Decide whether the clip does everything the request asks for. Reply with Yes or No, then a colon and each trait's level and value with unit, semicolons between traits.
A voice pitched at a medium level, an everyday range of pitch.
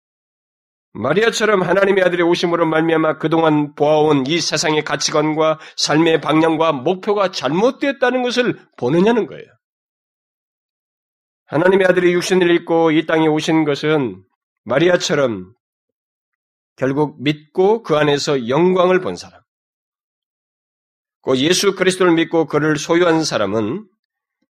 Yes: medium, 165 Hz; average, 3.3 semitones